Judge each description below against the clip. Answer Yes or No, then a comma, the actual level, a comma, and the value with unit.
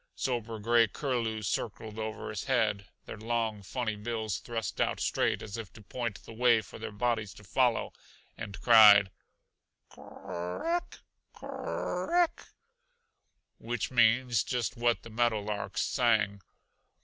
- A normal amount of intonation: No, narrow, 2.3 semitones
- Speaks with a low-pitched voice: Yes, low, 115 Hz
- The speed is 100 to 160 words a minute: Yes, average, 145 wpm